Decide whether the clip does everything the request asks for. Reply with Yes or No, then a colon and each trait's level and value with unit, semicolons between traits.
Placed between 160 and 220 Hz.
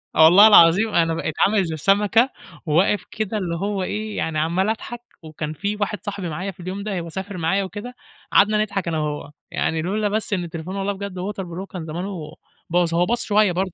Yes: high, 190 Hz